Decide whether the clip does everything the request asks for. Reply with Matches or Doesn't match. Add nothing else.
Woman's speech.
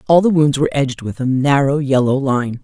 Matches